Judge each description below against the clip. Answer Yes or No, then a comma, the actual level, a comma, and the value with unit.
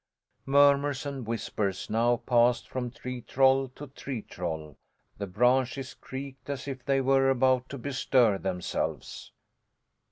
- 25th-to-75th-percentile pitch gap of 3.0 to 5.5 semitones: No, narrow, 2.6 semitones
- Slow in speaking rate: Yes, slow, 130 wpm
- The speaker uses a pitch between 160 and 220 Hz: No, low, 130 Hz